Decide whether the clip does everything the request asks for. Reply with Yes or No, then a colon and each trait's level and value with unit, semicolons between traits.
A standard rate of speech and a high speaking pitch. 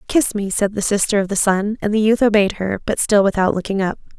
No: fast, 260 wpm; high, 205 Hz